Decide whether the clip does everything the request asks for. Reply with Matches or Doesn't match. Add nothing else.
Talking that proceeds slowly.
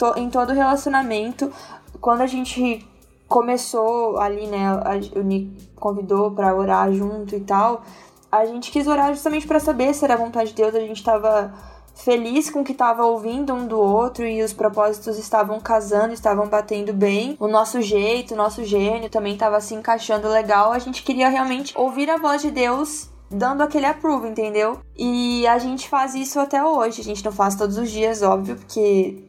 Doesn't match